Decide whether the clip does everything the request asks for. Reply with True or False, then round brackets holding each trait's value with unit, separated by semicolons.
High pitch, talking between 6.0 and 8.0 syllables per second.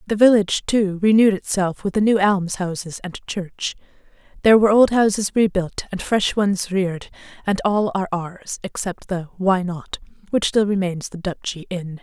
False (195 Hz; 5.0 syllables/s)